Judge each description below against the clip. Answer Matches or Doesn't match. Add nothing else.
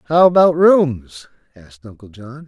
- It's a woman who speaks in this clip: Doesn't match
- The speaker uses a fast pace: Doesn't match